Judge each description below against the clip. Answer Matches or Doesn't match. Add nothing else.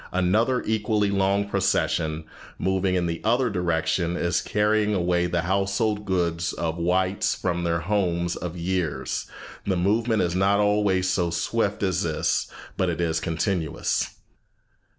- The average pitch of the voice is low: Matches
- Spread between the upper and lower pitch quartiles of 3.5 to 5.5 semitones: Doesn't match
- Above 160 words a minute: Doesn't match